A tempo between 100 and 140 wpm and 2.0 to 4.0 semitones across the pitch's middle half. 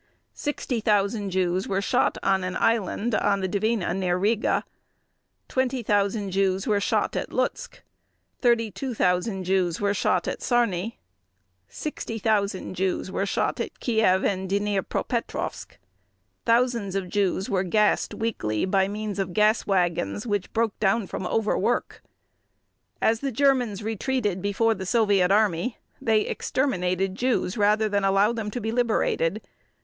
Yes: slow, 135 wpm; average, 3.0 semitones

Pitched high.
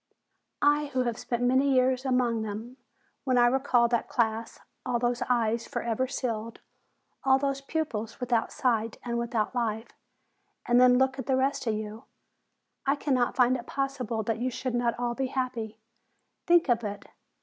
Yes: high, 245 Hz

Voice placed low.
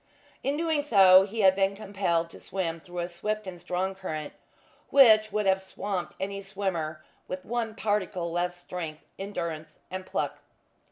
No: high, 190 Hz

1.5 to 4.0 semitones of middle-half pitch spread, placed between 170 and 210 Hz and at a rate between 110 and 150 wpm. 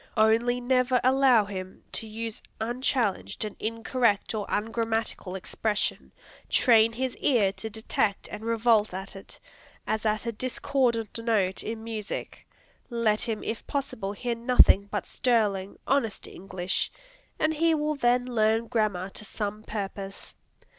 No: average, 2.7 semitones; high, 225 Hz; slow, 135 wpm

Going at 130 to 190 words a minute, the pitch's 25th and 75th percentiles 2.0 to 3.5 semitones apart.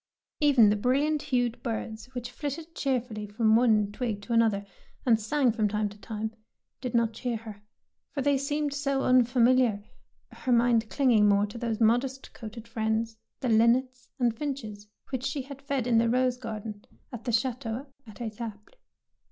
Yes: average, 175 wpm; average, 3.0 semitones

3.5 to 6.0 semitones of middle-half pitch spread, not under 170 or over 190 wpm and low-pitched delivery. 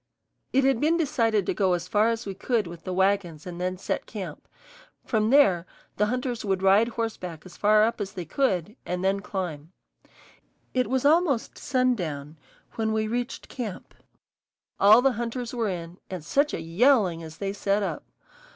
No: average, 4.9 semitones; average, 180 wpm; high, 205 Hz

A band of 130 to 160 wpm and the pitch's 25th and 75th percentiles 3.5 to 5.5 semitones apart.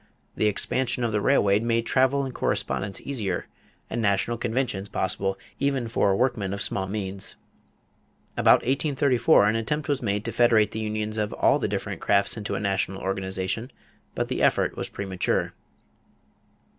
Yes: average, 155 wpm; average, 4.0 semitones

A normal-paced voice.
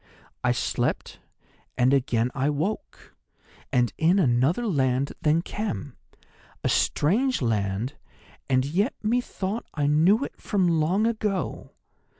No: slow, 115 wpm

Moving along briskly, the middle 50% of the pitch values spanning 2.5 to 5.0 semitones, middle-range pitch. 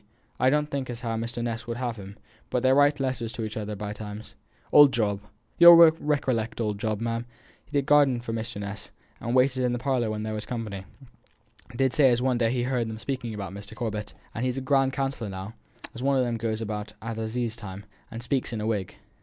No: fast, 230 wpm; average, 3.2 semitones; low, 115 Hz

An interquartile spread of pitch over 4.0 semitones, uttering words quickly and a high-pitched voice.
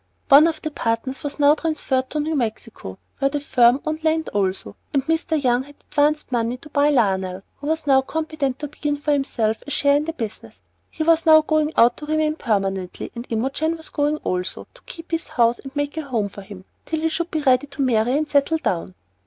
Yes: average, 4.7 semitones; fast, 220 wpm; very high, 285 Hz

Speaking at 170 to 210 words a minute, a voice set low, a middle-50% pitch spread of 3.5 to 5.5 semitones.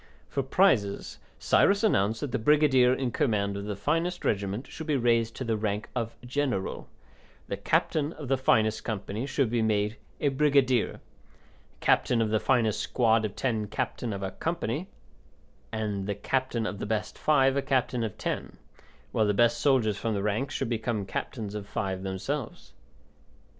Yes: average, 175 wpm; low, 115 Hz; average, 4.2 semitones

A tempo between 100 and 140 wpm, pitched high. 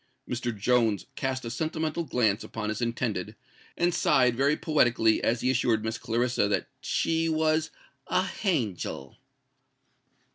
No: slow, 135 wpm; low, 125 Hz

